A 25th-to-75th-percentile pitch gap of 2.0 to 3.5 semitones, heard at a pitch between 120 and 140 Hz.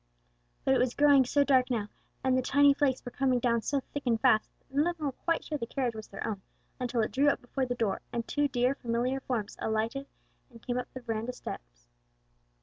No: average, 2.8 semitones; very high, 250 Hz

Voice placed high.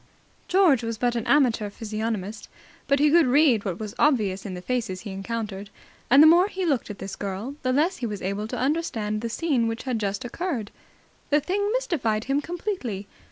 Yes: high, 235 Hz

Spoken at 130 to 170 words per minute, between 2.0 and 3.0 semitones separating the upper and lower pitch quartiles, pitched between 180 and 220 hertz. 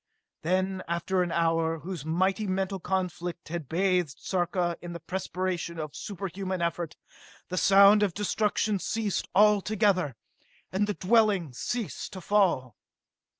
Yes: slow, 135 wpm; narrow, 2.6 semitones; medium, 185 Hz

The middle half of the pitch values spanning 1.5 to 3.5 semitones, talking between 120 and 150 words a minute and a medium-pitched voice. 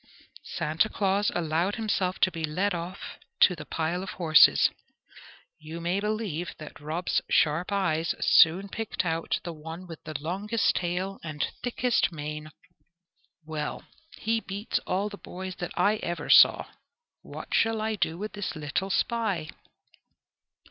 No: average, 4.0 semitones; average, 145 wpm; medium, 180 Hz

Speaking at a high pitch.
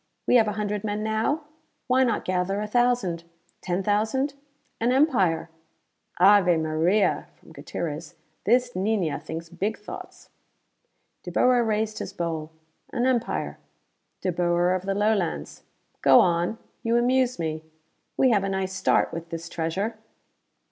Yes: high, 200 Hz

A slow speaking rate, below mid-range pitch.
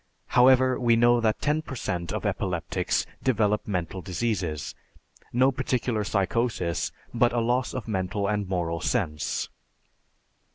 Yes: slow, 130 wpm; low, 110 Hz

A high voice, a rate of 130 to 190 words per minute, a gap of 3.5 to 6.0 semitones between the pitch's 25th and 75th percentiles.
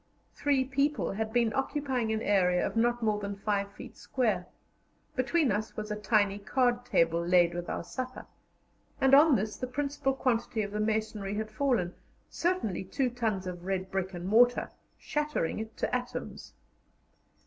Yes: high, 220 Hz; average, 165 wpm; average, 4.4 semitones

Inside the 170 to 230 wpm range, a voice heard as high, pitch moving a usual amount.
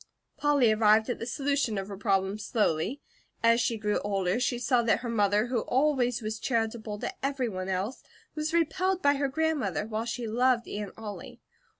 Yes: average, 180 wpm; high, 230 Hz; average, 4.0 semitones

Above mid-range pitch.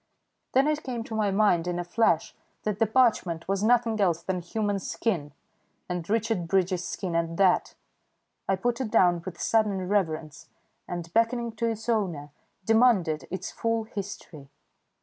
Yes: high, 195 Hz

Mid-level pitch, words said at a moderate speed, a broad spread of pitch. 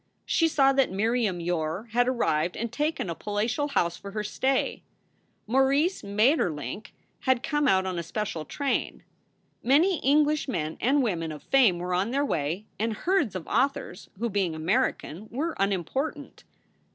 No: high, 225 Hz; average, 155 wpm; wide, 7.2 semitones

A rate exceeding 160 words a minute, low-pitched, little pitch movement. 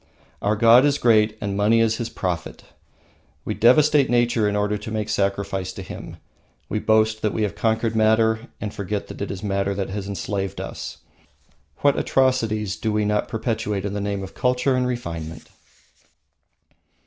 Yes: average, 170 wpm; low, 105 Hz; narrow, 2.2 semitones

